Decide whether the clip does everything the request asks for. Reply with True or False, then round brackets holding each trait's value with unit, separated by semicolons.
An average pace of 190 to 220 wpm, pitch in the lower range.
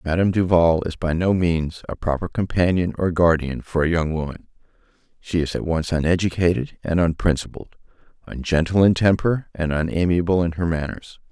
False (160 wpm; 85 Hz)